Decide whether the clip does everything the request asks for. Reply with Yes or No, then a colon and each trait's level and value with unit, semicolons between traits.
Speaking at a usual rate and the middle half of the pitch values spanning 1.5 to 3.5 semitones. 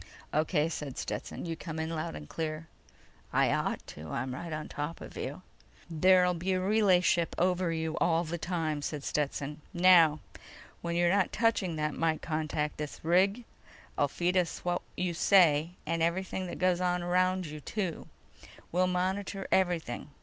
Yes: average, 170 wpm; average, 2.9 semitones